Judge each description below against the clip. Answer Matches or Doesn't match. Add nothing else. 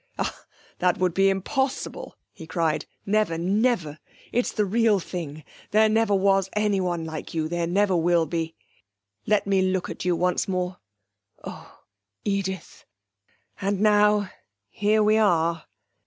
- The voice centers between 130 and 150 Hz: Doesn't match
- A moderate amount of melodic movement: Matches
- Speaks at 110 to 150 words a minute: Matches